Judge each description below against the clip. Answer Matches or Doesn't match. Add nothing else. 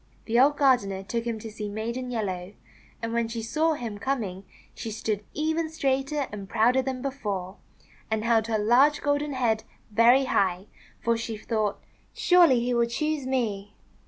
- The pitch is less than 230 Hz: Doesn't match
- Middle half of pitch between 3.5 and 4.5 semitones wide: Matches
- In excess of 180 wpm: Doesn't match